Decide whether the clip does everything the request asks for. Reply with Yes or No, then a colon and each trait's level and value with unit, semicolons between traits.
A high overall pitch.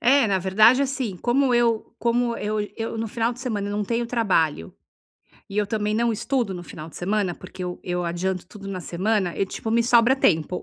Yes: high, 210 Hz